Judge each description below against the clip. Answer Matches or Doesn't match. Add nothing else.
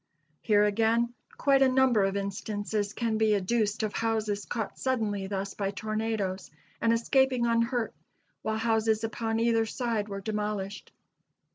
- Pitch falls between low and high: Doesn't match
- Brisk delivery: Doesn't match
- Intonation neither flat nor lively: Doesn't match